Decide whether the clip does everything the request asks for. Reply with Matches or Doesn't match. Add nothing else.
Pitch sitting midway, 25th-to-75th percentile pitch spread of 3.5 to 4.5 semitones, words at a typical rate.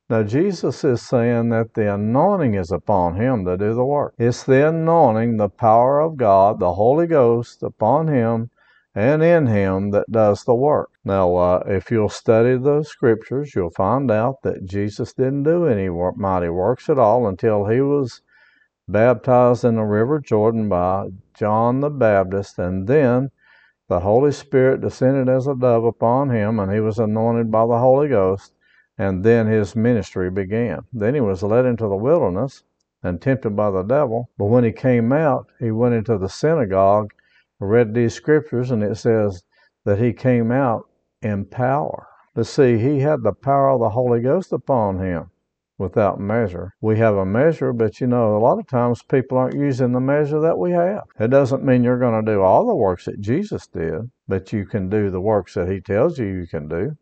Doesn't match